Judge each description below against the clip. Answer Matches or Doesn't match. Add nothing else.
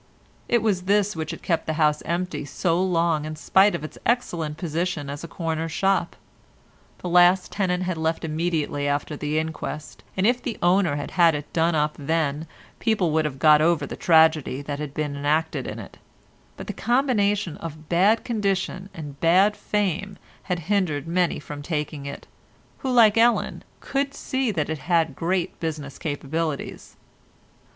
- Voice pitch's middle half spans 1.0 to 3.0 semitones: Doesn't match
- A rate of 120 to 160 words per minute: Doesn't match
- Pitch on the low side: Doesn't match